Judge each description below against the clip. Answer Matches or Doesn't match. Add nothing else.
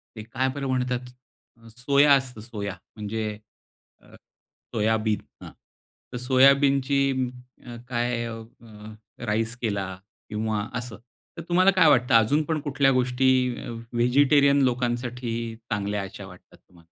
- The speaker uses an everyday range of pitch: Matches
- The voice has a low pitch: Matches